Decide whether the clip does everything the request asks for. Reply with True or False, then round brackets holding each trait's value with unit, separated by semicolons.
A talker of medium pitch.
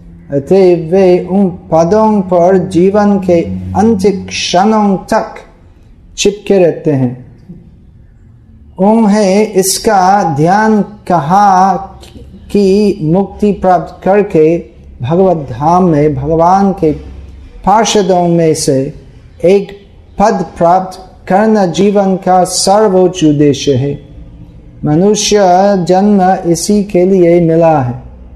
True (180 Hz)